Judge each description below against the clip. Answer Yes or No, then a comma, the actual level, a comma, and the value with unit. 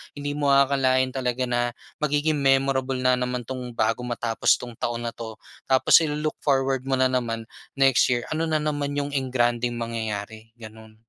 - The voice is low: Yes, low, 130 Hz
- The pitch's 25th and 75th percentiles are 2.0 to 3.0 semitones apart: Yes, narrow, 2.6 semitones